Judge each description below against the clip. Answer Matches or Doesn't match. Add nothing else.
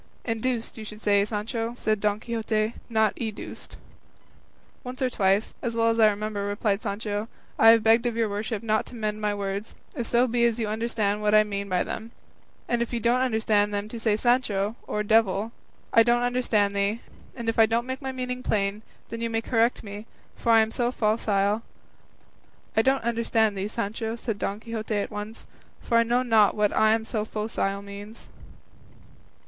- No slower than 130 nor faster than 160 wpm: Doesn't match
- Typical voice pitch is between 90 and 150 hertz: Doesn't match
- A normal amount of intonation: Doesn't match